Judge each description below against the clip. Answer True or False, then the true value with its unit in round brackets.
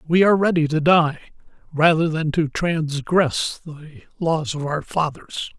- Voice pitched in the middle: True (160 Hz)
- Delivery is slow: False (150 wpm)